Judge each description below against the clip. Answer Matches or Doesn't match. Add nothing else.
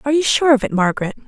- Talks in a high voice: Matches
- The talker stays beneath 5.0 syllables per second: Doesn't match